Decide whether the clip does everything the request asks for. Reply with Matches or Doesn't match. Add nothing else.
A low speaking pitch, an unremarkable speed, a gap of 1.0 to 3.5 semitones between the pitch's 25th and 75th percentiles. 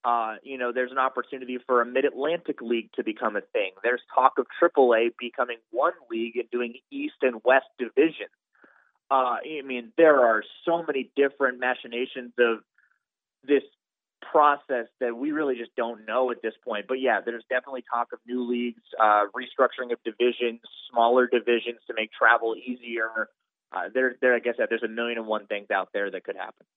Matches